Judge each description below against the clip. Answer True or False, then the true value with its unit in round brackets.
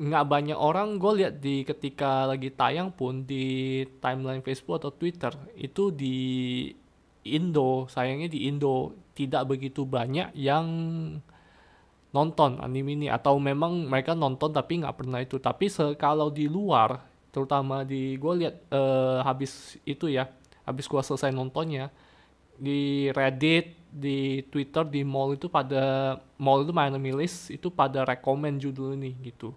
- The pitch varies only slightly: True (2.3 semitones)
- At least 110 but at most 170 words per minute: True (140 wpm)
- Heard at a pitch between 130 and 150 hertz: True (140 Hz)